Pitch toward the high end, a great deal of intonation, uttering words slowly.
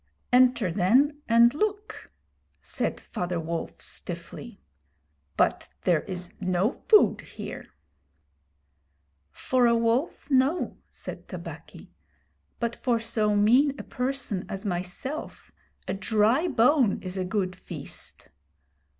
Yes: high, 230 Hz; wide, 6.0 semitones; slow, 110 wpm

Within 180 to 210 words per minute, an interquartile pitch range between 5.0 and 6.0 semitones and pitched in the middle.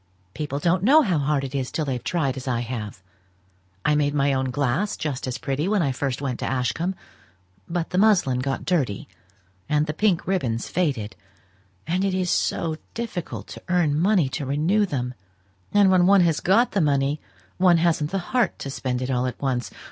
Yes: average, 195 wpm; wide, 5.4 semitones; medium, 150 Hz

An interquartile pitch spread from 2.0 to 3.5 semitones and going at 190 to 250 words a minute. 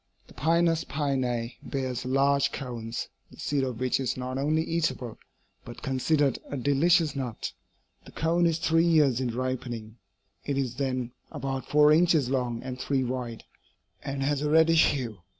No: average, 3.1 semitones; average, 160 wpm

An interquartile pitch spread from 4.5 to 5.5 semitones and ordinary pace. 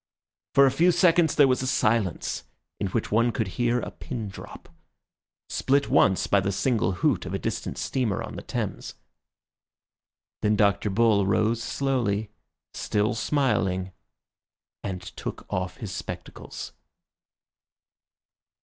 No: average, 5.0 semitones; slow, 130 wpm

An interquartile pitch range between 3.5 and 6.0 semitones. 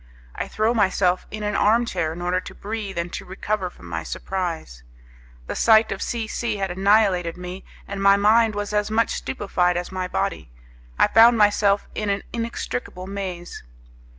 No: average, 3.1 semitones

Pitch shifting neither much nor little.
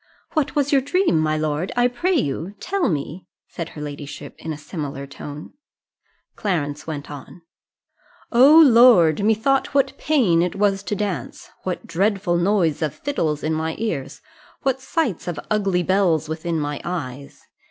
No: wide, 7.3 semitones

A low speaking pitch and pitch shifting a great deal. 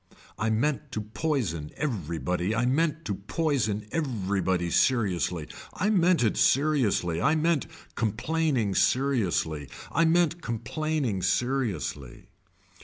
Yes: low, 115 Hz; wide, 8.1 semitones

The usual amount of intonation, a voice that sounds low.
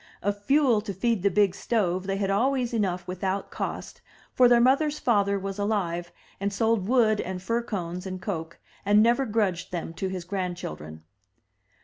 No: average, 3.8 semitones; high, 200 Hz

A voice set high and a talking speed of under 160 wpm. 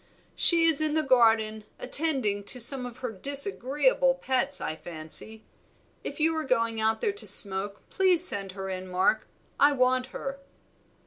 No: very high, 255 Hz; average, 165 wpm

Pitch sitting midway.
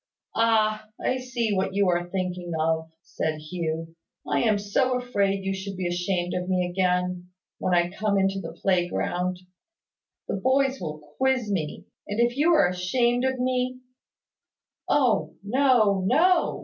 No: high, 195 Hz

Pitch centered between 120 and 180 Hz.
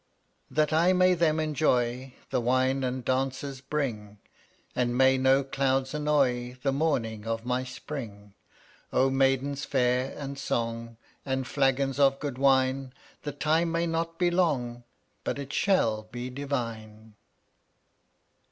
Yes: low, 135 Hz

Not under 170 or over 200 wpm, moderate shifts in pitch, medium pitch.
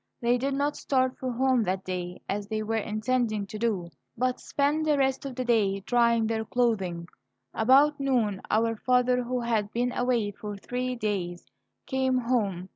No: average, 175 wpm; average, 3.6 semitones; high, 235 Hz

